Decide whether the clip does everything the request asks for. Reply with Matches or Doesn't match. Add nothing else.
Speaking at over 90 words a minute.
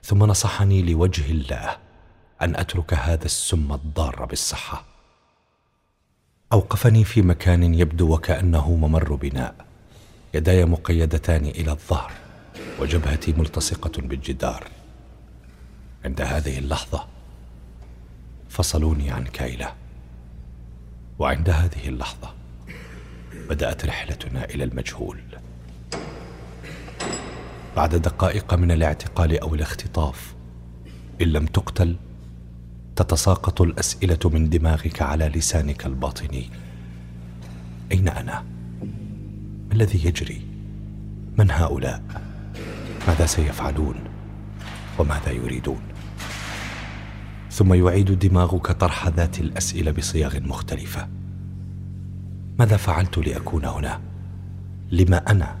Doesn't match